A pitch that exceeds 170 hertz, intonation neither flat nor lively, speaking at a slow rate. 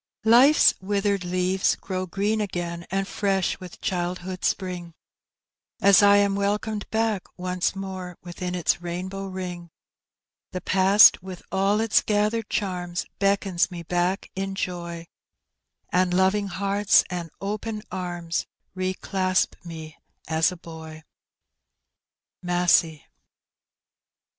No: medium, 185 Hz; narrow, 2.2 semitones; slow, 115 wpm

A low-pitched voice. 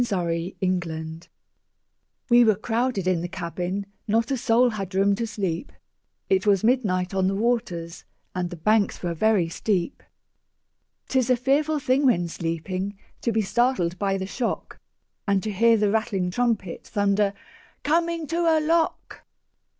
No: high, 205 Hz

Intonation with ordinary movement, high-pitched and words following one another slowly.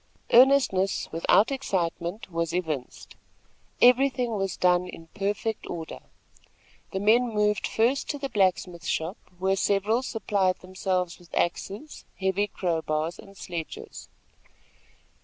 Yes: average, 4.1 semitones; high, 195 Hz; slow, 120 wpm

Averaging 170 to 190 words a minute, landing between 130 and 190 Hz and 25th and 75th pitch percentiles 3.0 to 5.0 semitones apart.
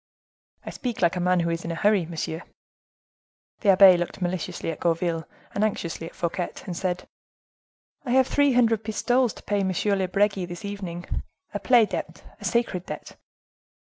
Yes: average, 180 wpm; medium, 185 Hz; average, 3.6 semitones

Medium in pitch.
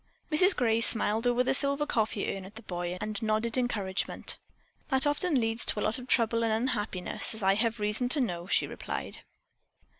No: high, 225 Hz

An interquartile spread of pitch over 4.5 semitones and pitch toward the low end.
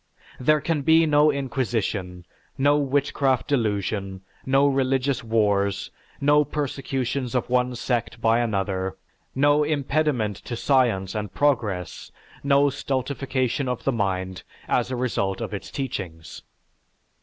Yes: average, 5.3 semitones; low, 125 Hz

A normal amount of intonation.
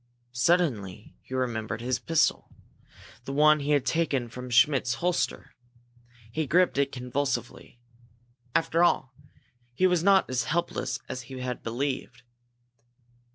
Yes: average, 4.3 semitones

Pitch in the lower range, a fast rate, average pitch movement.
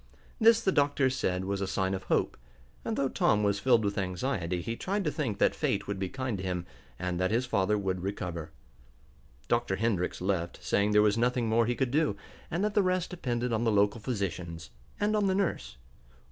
No: low, 105 Hz; fast, 210 wpm; wide, 5.7 semitones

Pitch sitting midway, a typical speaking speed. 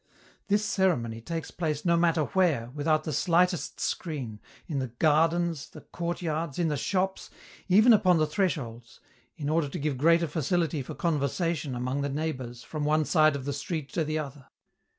Yes: medium, 155 Hz; average, 170 wpm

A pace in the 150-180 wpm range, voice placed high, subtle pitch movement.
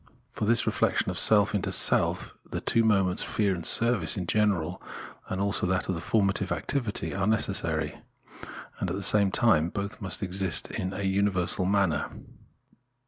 No: average, 155 wpm; very low, 95 Hz; narrow, 2.2 semitones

